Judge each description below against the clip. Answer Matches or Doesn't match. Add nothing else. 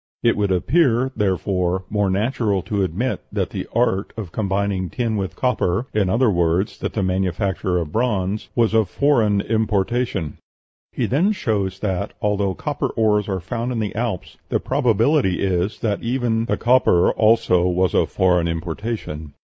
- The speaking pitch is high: Doesn't match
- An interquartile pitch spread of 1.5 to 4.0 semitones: Matches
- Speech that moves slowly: Doesn't match